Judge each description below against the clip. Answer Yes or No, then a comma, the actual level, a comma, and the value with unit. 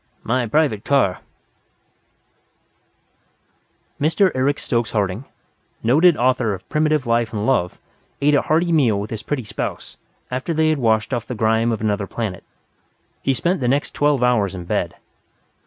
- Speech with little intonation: No, average, 5.0 semitones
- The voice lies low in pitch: Yes, low, 125 Hz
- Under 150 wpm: No, average, 155 wpm